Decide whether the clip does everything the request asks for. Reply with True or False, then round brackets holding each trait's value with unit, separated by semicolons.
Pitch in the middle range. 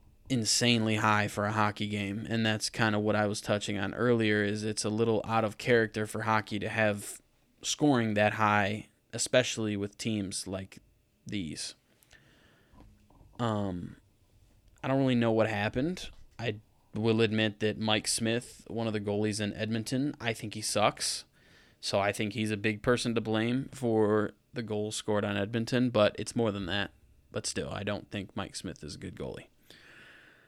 False (110 Hz)